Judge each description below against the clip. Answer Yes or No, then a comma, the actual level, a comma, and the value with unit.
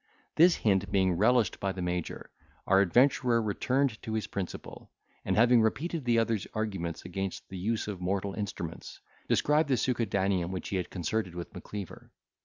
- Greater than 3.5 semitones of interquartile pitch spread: Yes, average, 3.9 semitones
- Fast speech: No, average, 165 wpm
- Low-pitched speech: Yes, low, 100 Hz